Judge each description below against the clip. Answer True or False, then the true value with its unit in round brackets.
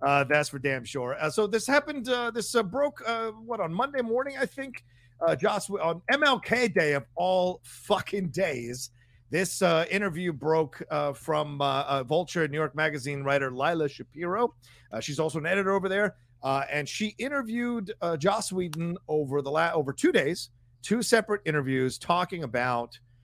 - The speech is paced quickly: False (180 wpm)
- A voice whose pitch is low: False (165 Hz)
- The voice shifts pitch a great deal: True (7.0 semitones)